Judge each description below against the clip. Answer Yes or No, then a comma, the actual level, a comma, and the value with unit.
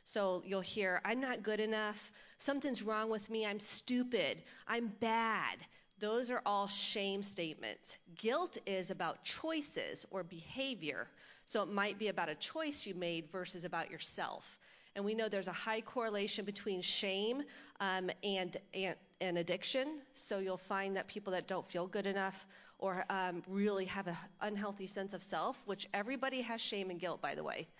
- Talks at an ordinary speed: Yes, average, 175 wpm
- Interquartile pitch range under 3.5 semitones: Yes, average, 3.0 semitones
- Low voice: No, high, 200 Hz